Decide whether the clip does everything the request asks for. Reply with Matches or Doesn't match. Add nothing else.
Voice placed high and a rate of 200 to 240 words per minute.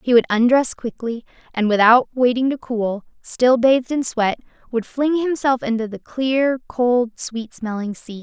Doesn't match